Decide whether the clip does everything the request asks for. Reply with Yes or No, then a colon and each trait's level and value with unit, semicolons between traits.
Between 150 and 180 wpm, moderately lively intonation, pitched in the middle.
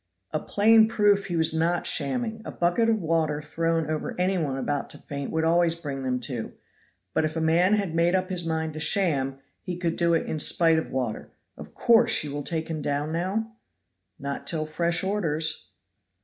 No: average, 200 wpm; average, 3.3 semitones; medium, 165 Hz